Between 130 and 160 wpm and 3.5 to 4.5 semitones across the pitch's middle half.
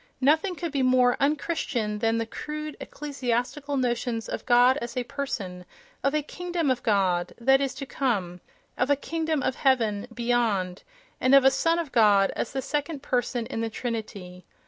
No: average, 180 wpm; average, 4.0 semitones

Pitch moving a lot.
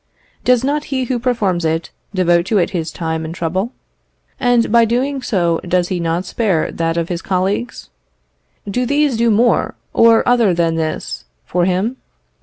Yes: wide, 5.9 semitones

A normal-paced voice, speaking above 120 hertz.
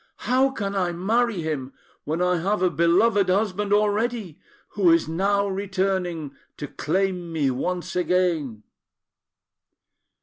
No: slow, 125 wpm; medium, 185 Hz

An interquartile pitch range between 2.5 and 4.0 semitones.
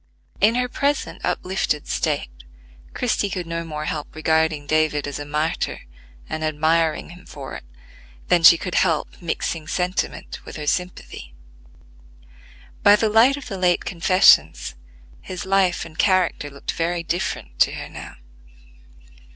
Yes: average, 3.3 semitones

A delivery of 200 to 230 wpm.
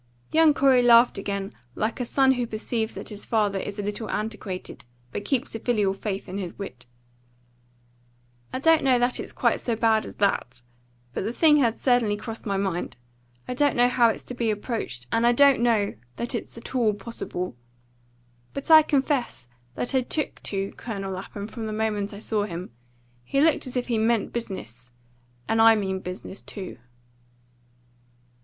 No: average, 180 wpm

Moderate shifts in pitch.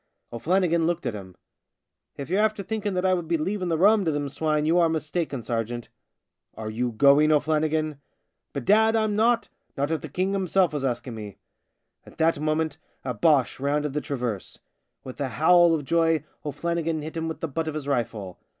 Yes: average, 3.8 semitones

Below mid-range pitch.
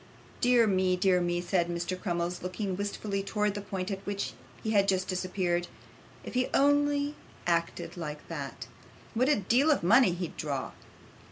No: high, 190 Hz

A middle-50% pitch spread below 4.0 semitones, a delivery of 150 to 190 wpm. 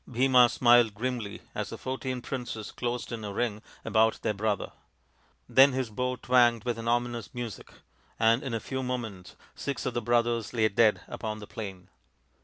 Yes: narrow, 2.4 semitones; average, 175 wpm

